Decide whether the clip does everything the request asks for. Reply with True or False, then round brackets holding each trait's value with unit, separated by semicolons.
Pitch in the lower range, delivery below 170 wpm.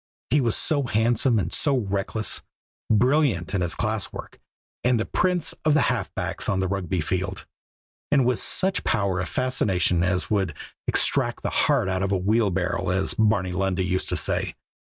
False (100 Hz; 175 wpm)